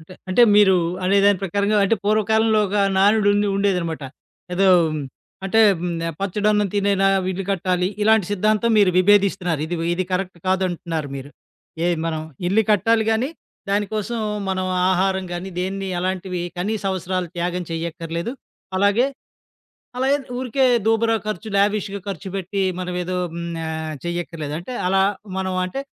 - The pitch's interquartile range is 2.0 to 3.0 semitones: Yes, average, 2.7 semitones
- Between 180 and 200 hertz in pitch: Yes, high, 190 Hz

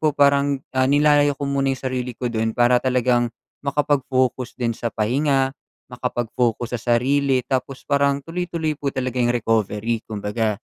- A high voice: No, low, 130 Hz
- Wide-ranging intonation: No, average, 2.7 semitones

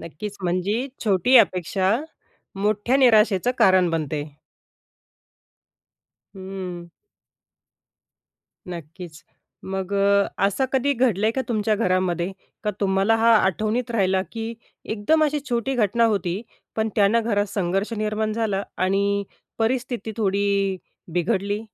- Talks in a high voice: Yes, high, 200 Hz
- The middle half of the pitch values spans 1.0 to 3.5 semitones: Yes, average, 3.1 semitones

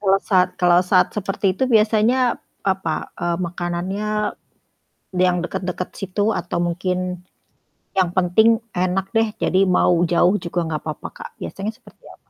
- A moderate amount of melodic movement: No, narrow, 2.1 semitones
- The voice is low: No, medium, 185 Hz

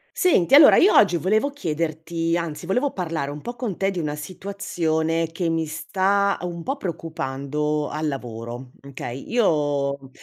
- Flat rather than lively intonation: No, average, 4.5 semitones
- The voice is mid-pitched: Yes, medium, 165 Hz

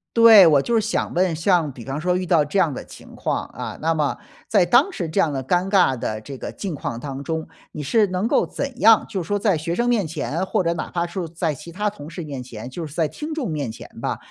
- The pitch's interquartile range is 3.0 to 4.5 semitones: No, average, 5.1 semitones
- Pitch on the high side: No, medium, 170 Hz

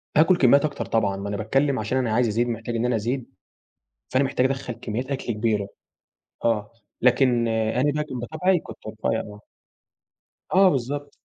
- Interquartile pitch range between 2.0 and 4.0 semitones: Yes, average, 3.6 semitones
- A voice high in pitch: No, low, 125 Hz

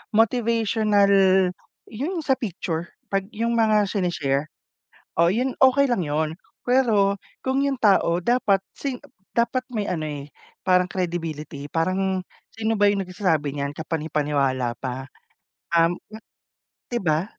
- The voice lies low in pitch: No, high, 195 Hz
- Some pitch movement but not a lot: No, wide, 6.3 semitones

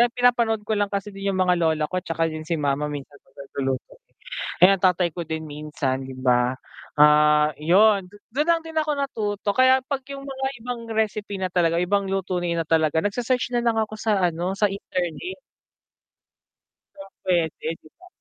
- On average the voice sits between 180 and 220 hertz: Yes, high, 190 Hz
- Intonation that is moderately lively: No, wide, 5.9 semitones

